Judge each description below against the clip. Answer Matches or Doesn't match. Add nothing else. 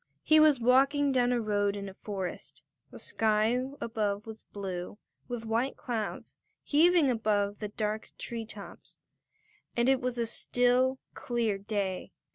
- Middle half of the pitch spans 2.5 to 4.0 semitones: Matches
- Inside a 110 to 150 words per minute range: Matches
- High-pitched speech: Matches